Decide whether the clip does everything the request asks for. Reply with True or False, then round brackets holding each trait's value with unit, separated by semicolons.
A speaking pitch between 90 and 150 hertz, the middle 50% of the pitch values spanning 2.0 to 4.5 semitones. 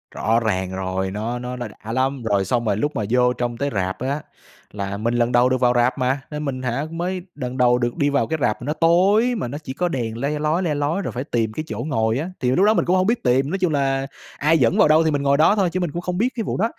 False (135 Hz; 5.0 semitones)